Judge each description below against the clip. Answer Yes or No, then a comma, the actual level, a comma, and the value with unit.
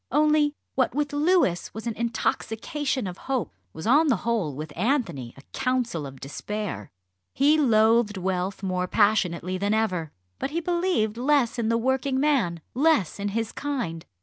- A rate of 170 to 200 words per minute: No, average, 160 wpm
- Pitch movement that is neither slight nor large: No, wide, 7.0 semitones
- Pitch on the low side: No, high, 225 Hz